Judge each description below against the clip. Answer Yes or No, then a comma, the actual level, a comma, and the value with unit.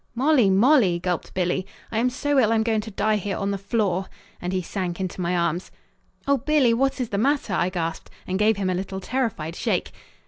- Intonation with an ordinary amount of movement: Yes, average, 4.6 semitones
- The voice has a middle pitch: No, high, 200 Hz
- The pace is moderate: No, fast, 215 wpm